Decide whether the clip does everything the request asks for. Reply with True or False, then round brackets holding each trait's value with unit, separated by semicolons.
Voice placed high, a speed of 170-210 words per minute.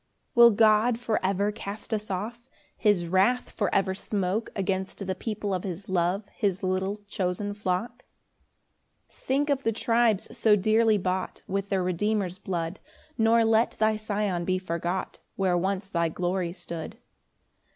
False (200 Hz; 155 wpm)